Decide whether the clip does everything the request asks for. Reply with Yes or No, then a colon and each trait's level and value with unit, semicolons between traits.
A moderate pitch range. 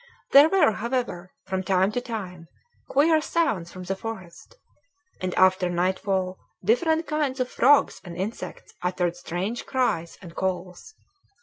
No: wide, 6.1 semitones